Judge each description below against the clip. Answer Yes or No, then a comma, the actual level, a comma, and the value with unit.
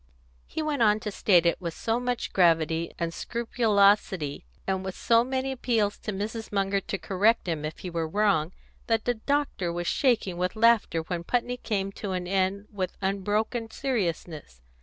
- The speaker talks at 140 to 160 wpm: No, average, 175 wpm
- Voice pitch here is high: Yes, high, 200 Hz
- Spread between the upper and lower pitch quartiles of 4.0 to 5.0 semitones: Yes, average, 4.6 semitones